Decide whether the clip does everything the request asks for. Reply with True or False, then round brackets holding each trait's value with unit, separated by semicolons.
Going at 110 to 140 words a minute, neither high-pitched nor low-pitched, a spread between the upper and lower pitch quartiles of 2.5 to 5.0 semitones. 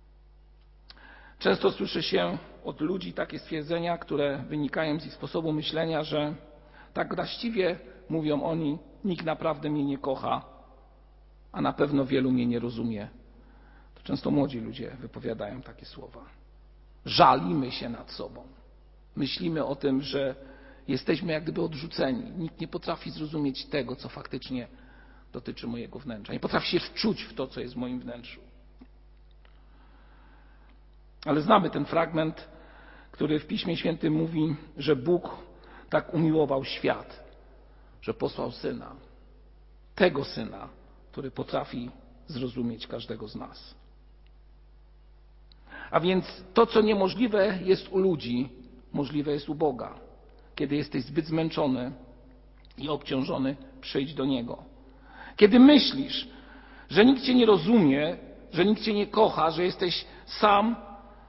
False (125 wpm; 150 Hz; 5.4 semitones)